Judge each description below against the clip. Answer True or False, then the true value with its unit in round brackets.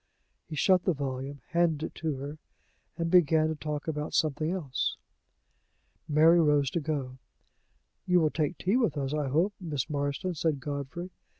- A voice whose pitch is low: False (155 Hz)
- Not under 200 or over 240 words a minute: False (165 wpm)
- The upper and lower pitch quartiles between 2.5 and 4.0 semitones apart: True (2.9 semitones)